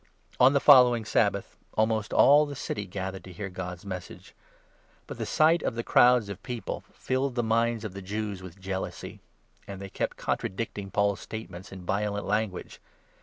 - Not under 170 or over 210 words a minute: Yes, average, 185 wpm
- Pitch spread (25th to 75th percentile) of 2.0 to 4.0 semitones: Yes, average, 3.6 semitones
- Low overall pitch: Yes, low, 105 Hz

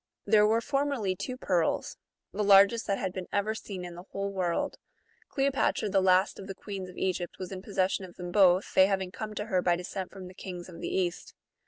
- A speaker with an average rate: No, fast, 220 wpm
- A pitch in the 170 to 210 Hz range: Yes, high, 190 Hz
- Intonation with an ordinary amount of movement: No, narrow, 2.3 semitones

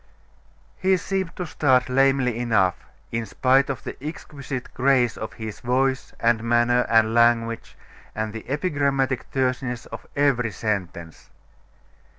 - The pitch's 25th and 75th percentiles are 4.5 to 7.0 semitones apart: No, average, 3.0 semitones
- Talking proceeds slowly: Yes, slow, 130 wpm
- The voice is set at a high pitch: No, low, 125 Hz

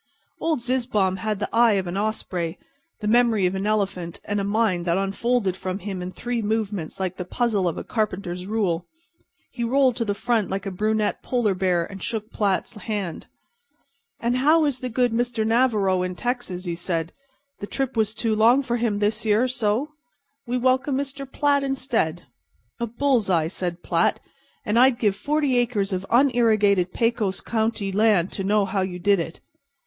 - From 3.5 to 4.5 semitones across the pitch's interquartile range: Yes, average, 4.2 semitones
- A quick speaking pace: No, average, 185 wpm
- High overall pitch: Yes, high, 215 Hz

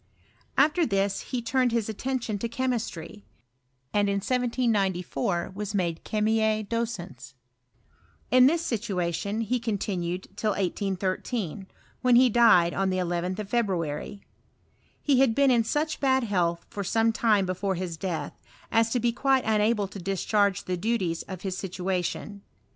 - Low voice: No, high, 205 Hz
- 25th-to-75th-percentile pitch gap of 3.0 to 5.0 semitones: Yes, average, 4.1 semitones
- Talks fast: No, average, 145 wpm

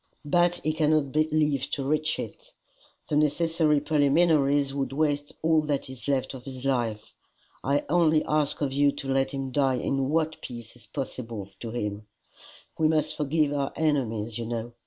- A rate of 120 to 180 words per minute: Yes, average, 170 wpm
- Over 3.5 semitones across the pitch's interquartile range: No, average, 2.8 semitones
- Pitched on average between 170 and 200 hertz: No, medium, 140 Hz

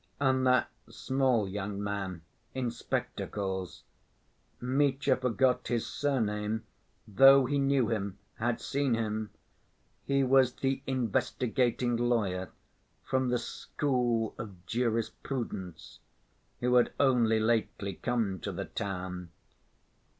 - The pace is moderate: No, slow, 105 wpm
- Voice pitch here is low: Yes, low, 120 Hz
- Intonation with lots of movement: No, average, 4.0 semitones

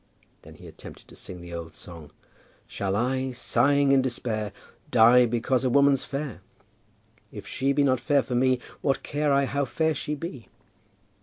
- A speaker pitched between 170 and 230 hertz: No, low, 130 Hz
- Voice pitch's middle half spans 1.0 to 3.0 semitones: No, average, 3.4 semitones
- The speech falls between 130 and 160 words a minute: No, average, 170 wpm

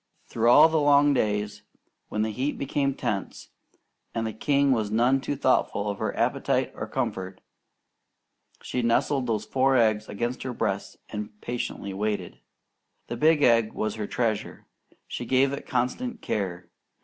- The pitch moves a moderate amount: Yes, average, 4.3 semitones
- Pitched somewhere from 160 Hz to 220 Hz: No, low, 120 Hz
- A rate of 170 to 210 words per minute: No, average, 155 wpm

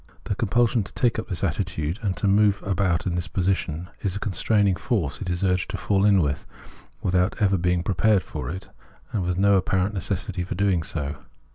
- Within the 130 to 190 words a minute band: No, average, 200 wpm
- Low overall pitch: Yes, very low, 95 Hz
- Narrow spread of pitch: Yes, narrow, 2.3 semitones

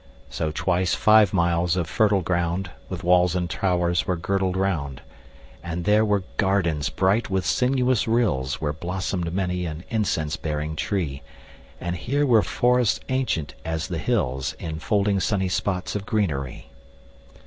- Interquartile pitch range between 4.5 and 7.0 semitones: No, average, 3.7 semitones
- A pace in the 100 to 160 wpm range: Yes, average, 150 wpm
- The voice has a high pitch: No, very low, 90 Hz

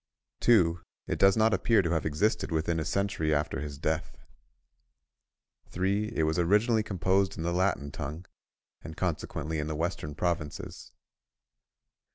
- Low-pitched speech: Yes, very low, 85 Hz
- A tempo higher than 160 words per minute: No, average, 145 wpm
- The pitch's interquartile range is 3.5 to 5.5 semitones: Yes, average, 3.9 semitones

